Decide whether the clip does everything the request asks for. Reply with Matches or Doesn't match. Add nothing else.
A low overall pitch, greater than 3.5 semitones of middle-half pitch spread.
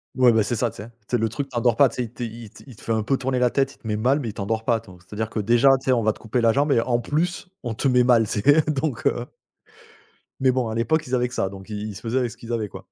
Doesn't match